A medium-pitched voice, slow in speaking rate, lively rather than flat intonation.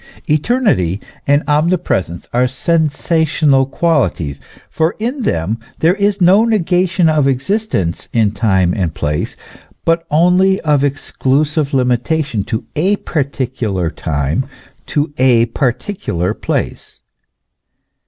Yes: medium, 145 Hz; slow, 105 wpm; wide, 7.0 semitones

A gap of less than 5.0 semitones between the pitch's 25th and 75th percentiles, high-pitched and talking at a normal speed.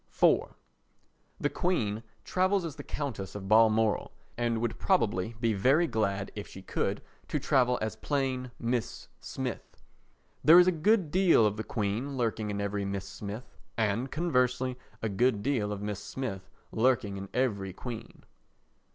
No: average, 4.4 semitones; low, 115 Hz; average, 155 wpm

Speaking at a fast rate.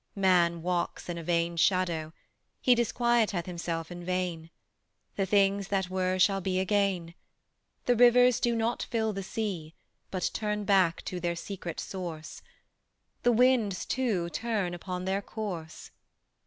No: average, 140 wpm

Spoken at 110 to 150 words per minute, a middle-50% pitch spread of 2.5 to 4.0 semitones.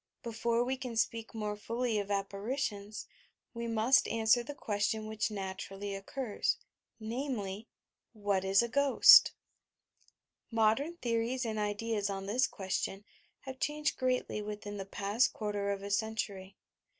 Yes: average, 140 wpm; average, 2.8 semitones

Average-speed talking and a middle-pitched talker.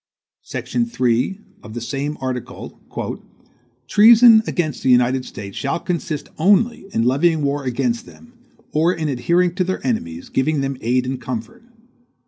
Yes: average, 145 wpm; medium, 155 Hz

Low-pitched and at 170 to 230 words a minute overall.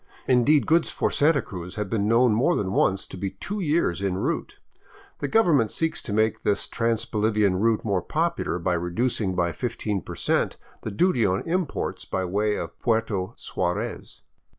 Yes: low, 110 Hz; average, 175 wpm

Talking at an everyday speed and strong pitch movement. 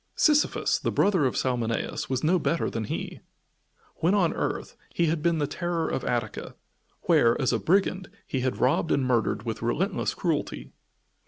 Yes: average, 170 wpm; wide, 5.7 semitones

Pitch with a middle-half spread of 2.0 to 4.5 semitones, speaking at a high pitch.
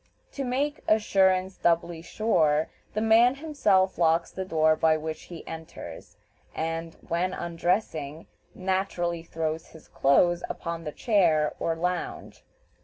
No: average, 2.9 semitones; medium, 170 Hz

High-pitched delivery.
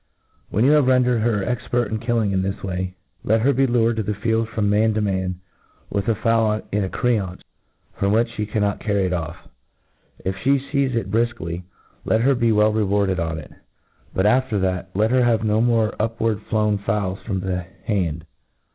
No: low, 105 Hz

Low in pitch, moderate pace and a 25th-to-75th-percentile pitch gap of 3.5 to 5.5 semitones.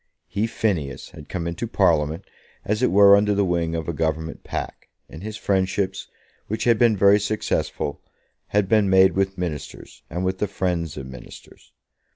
Yes: very low, 95 Hz; average, 175 wpm; average, 3.8 semitones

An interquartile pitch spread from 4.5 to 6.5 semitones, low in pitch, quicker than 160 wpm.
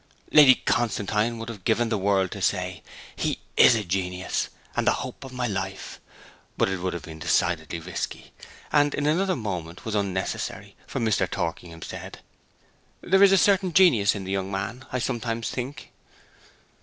Yes: average, 5.1 semitones; low, 105 Hz; average, 170 wpm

